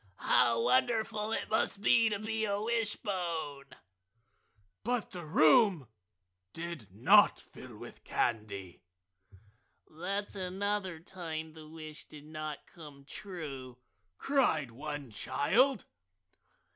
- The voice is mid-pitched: Yes, medium, 165 Hz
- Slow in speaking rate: Yes, slow, 105 wpm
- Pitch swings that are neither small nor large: No, wide, 6.2 semitones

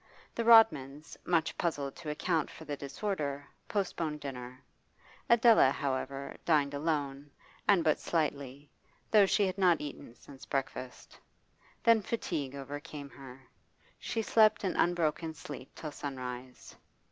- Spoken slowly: Yes, slow, 125 wpm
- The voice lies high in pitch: No, medium, 150 Hz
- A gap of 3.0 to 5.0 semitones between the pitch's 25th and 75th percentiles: Yes, average, 4.1 semitones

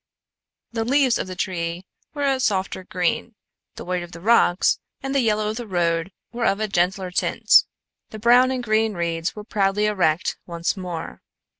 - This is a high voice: Yes, high, 195 Hz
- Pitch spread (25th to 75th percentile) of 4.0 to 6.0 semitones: Yes, average, 4.7 semitones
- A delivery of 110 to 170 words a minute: No, average, 180 wpm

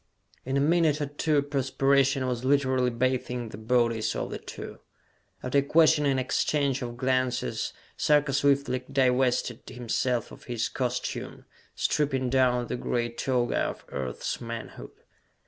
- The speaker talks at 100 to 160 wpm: Yes, average, 140 wpm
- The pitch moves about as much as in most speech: No, narrow, 2.2 semitones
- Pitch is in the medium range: No, low, 130 Hz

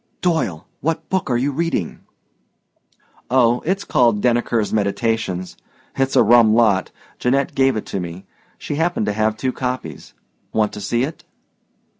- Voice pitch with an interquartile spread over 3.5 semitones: Yes, average, 4.2 semitones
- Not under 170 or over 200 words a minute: No, average, 150 wpm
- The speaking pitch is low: Yes, low, 120 Hz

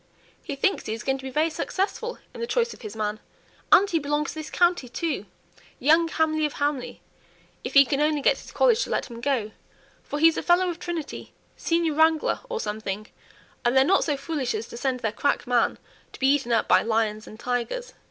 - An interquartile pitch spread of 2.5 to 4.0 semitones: No, average, 5.3 semitones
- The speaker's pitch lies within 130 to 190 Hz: No, very high, 290 Hz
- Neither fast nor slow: No, fast, 220 wpm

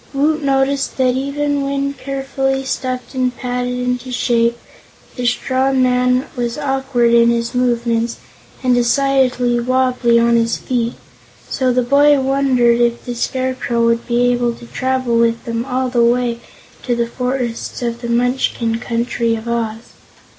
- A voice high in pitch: Yes, very high, 250 Hz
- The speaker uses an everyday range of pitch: No, narrow, 1.9 semitones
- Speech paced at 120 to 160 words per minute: Yes, average, 150 wpm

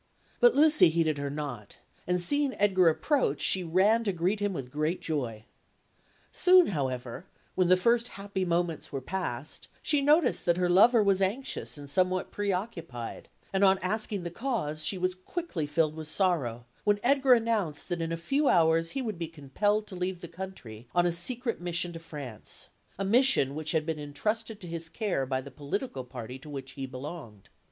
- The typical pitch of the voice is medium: Yes, medium, 175 Hz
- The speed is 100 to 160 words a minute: No, average, 185 wpm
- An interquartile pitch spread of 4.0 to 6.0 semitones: Yes, wide, 5.6 semitones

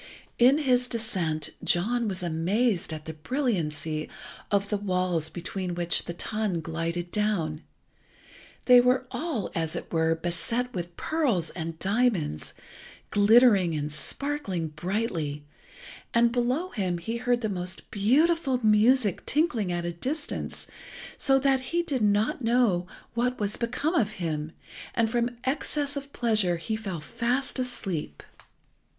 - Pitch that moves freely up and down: Yes, wide, 6.4 semitones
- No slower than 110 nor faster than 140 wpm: Yes, slow, 135 wpm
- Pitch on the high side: Yes, high, 210 Hz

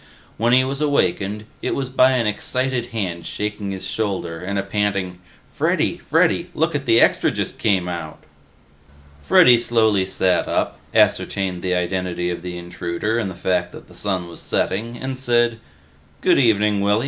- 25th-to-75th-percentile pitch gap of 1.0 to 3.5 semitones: No, average, 4.5 semitones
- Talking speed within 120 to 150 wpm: No, average, 165 wpm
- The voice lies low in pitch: Yes, low, 100 Hz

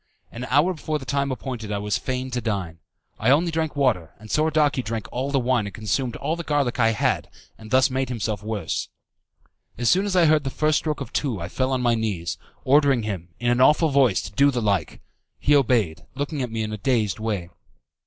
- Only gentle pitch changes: No, average, 4.8 semitones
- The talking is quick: Yes, fast, 220 wpm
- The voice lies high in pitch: No, low, 125 Hz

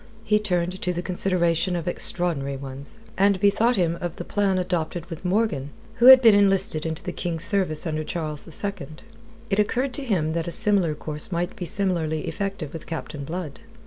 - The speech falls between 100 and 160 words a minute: No, average, 185 wpm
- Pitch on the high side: No, medium, 175 Hz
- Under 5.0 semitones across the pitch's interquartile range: Yes, average, 3.8 semitones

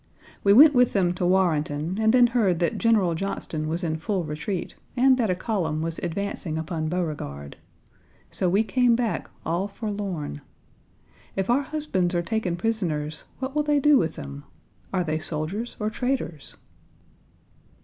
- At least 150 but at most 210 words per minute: Yes, average, 160 wpm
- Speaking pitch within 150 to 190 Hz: Yes, medium, 185 Hz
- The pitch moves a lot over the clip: Yes, wide, 5.9 semitones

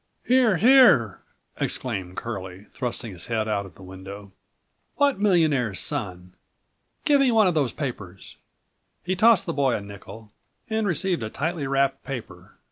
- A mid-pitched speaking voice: No, low, 130 Hz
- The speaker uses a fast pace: No, average, 150 wpm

